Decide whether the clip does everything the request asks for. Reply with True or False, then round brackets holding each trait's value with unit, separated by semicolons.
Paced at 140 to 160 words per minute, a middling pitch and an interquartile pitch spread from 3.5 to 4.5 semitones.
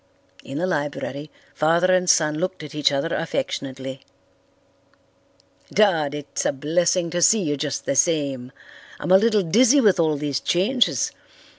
True (150 wpm; 160 Hz; 4.2 semitones)